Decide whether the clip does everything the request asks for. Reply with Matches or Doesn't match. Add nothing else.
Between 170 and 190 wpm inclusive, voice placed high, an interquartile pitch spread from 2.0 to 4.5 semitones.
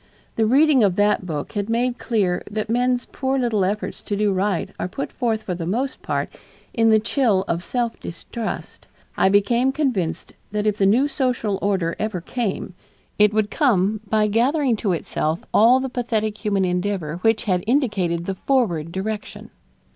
Matches